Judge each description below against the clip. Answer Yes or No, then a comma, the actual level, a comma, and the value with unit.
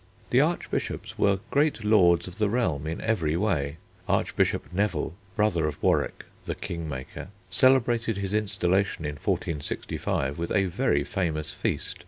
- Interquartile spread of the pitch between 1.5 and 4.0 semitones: No, wide, 5.4 semitones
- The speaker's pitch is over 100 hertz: No, very low, 90 Hz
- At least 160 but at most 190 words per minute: No, average, 145 wpm